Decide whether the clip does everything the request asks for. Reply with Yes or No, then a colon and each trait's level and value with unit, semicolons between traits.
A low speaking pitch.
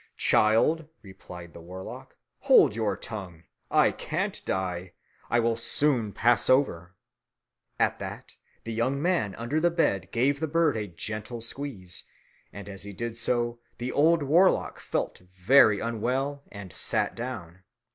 Yes: low, 115 Hz